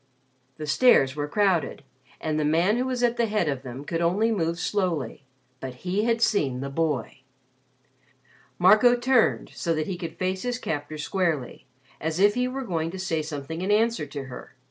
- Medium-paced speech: Yes, average, 190 wpm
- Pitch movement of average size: No, wide, 5.9 semitones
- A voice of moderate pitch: Yes, medium, 170 Hz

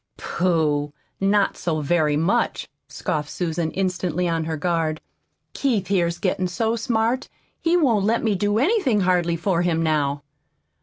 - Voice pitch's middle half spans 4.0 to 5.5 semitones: Yes, average, 4.4 semitones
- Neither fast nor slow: Yes, average, 145 wpm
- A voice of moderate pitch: Yes, medium, 180 Hz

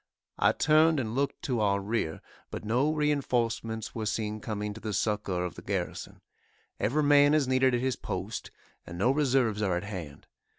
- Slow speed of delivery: No, average, 180 wpm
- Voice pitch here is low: Yes, low, 115 Hz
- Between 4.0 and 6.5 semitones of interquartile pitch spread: Yes, average, 4.5 semitones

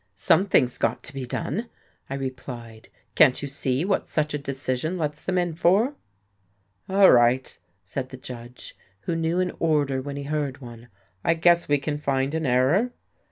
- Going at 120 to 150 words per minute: No, average, 170 wpm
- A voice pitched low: No, medium, 145 Hz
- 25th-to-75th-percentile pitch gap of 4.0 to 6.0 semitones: Yes, average, 4.4 semitones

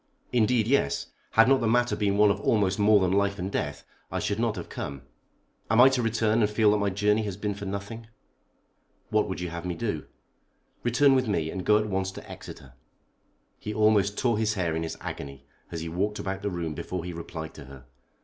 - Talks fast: Yes, fast, 220 wpm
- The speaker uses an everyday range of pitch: Yes, average, 3.8 semitones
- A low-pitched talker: Yes, low, 100 Hz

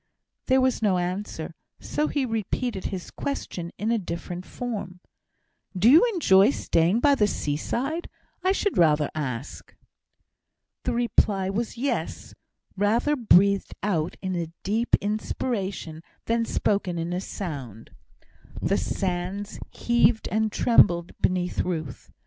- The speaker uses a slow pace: Yes, slow, 125 wpm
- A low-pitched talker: No, high, 200 Hz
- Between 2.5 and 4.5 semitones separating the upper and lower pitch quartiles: No, average, 5.0 semitones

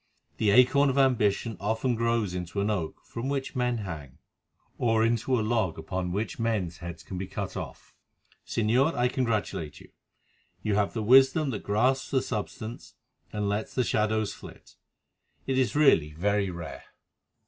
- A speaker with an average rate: Yes, average, 160 wpm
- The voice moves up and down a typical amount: Yes, average, 4.0 semitones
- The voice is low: Yes, low, 110 Hz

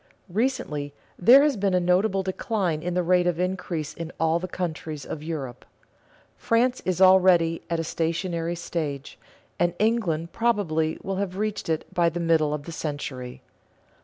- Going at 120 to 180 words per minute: Yes, average, 160 wpm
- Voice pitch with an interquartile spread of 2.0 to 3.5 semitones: Yes, average, 3.0 semitones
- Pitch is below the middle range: No, medium, 175 Hz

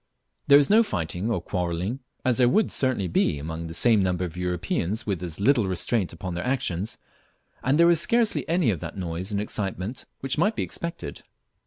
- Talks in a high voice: No, low, 100 Hz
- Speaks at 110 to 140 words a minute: No, average, 195 wpm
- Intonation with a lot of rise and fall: Yes, wide, 6.9 semitones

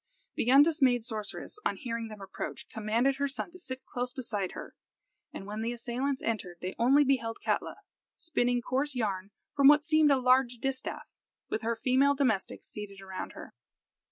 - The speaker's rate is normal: Yes, average, 170 wpm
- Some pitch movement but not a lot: Yes, average, 3.8 semitones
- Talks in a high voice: Yes, high, 245 Hz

